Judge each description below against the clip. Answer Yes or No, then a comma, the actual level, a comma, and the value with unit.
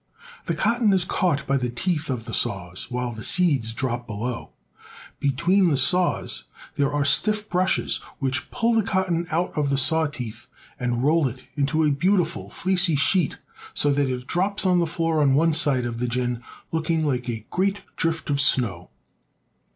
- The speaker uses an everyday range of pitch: No, wide, 5.9 semitones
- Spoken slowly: No, average, 180 wpm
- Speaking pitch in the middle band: Yes, medium, 145 Hz